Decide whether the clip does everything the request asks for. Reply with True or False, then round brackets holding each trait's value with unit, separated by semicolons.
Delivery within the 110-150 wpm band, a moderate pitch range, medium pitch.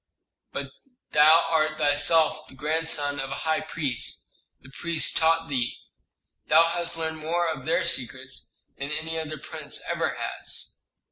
False (145 wpm; 2.1 semitones; 155 Hz)